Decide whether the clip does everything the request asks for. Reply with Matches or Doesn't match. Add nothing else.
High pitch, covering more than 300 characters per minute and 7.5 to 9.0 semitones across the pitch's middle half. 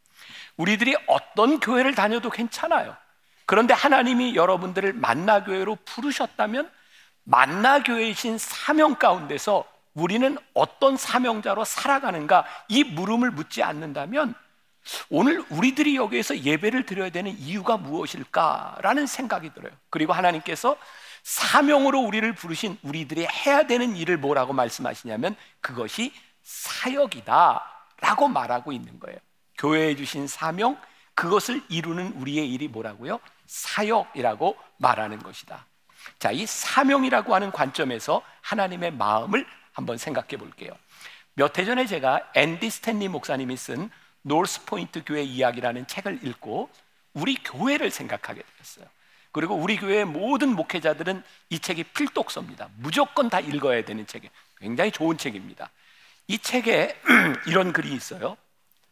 Matches